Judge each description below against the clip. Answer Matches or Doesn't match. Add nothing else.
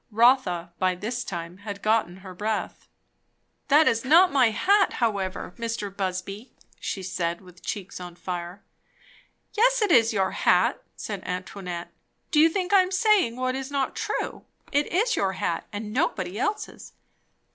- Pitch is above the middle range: Matches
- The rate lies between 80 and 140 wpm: Doesn't match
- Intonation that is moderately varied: Doesn't match